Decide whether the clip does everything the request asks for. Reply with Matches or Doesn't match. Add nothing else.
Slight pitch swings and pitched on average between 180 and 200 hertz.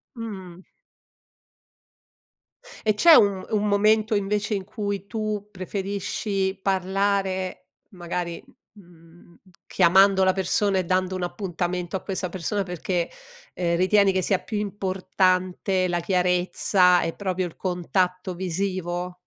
Matches